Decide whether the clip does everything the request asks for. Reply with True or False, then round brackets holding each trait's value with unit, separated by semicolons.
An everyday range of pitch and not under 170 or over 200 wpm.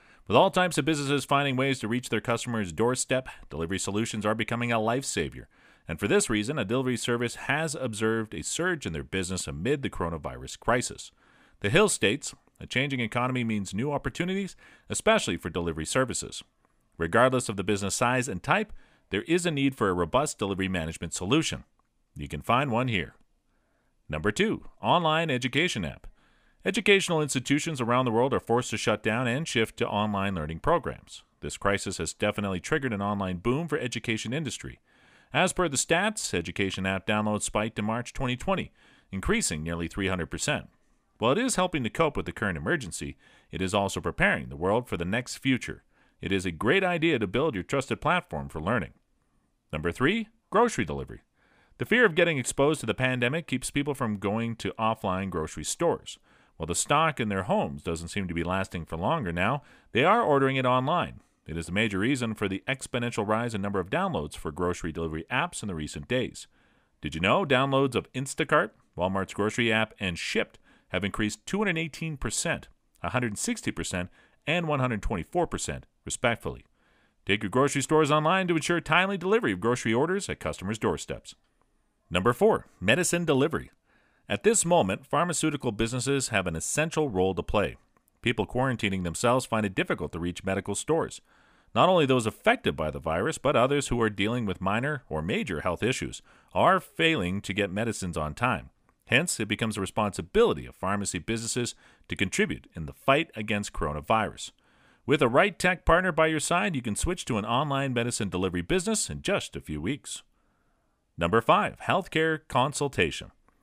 False (6.8 semitones; 175 wpm)